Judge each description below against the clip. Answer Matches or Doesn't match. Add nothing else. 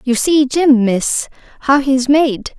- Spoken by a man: Doesn't match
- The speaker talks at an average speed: Matches